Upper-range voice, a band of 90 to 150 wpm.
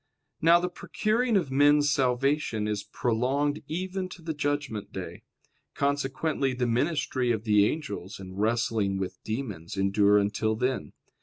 No: low, 130 Hz; average, 140 wpm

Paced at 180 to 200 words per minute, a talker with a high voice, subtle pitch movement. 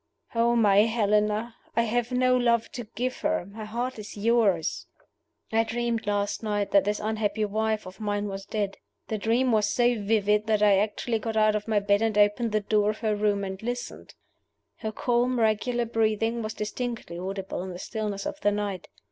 Yes: average, 190 wpm; high, 215 Hz; narrow, 2.1 semitones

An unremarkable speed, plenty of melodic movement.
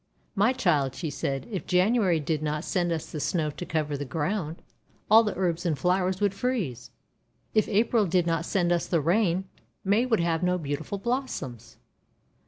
No: average, 185 wpm; average, 4.6 semitones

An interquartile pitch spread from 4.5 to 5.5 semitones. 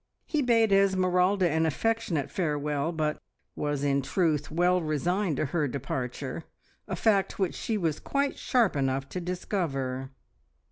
Yes: average, 5.1 semitones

